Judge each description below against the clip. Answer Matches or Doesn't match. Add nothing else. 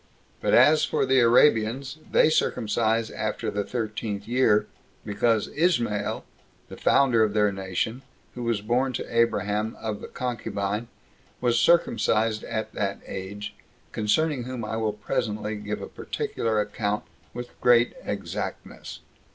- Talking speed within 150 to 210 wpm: Doesn't match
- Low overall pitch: Matches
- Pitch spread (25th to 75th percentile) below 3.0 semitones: Matches